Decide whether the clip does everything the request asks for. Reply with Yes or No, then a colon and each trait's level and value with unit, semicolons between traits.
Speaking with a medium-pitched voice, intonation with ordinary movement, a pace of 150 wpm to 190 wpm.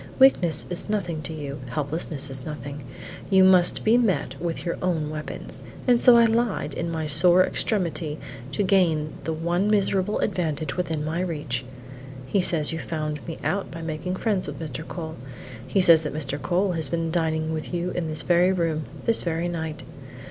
Yes: medium, 165 Hz; average, 3.0 semitones; average, 185 wpm